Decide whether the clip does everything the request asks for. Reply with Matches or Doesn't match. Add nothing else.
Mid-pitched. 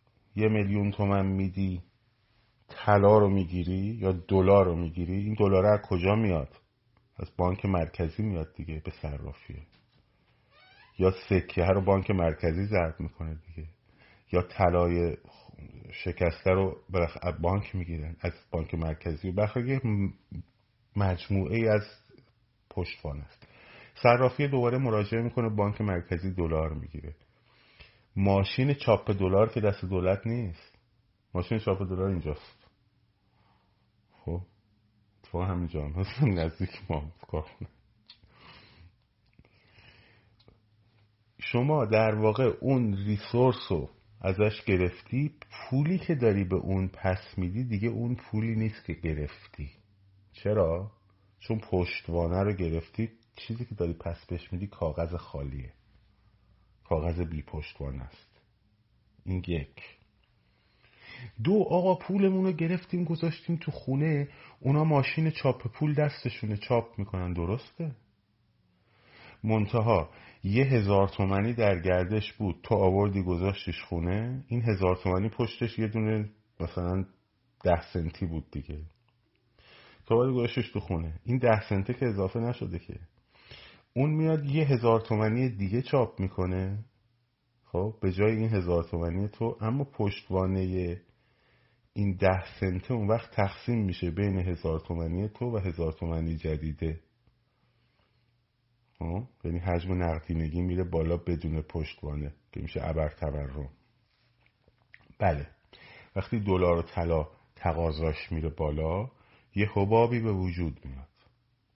Doesn't match